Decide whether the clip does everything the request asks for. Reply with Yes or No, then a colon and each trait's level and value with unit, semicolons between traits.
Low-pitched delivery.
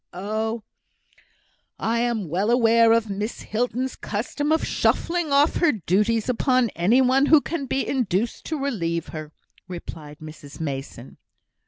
No: high, 230 Hz